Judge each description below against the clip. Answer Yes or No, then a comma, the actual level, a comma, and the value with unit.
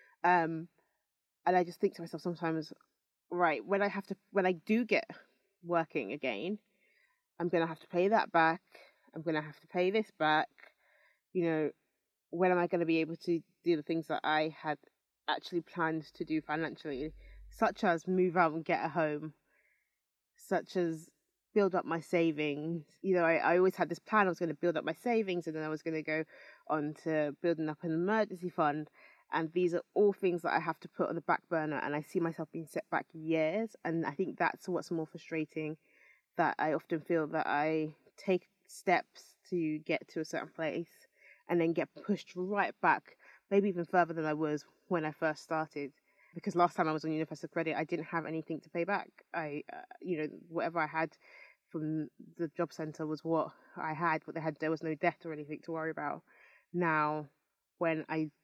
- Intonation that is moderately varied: No, narrow, 2.3 semitones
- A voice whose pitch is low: No, medium, 165 Hz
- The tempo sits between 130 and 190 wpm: No, fast, 205 wpm